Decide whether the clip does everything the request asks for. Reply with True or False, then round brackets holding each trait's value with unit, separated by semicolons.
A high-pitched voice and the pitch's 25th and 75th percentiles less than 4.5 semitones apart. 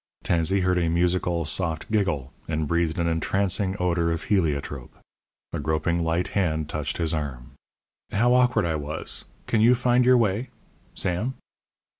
False (85 Hz; 4.0 semitones)